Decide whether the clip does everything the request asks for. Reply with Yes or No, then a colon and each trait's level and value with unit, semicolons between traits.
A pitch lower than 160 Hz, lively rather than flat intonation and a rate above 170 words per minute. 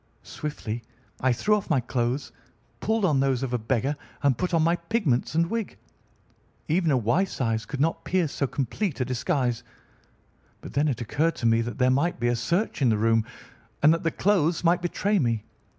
Yes: medium, 140 Hz; wide, 5.9 semitones; average, 200 wpm